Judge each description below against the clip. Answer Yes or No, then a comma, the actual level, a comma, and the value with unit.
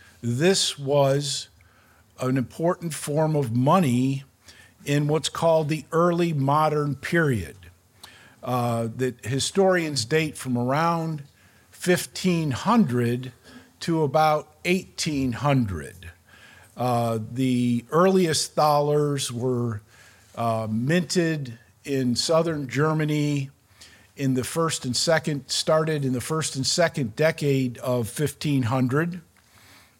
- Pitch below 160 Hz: Yes, medium, 140 Hz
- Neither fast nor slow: No, slow, 95 wpm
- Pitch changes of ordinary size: Yes, average, 4.7 semitones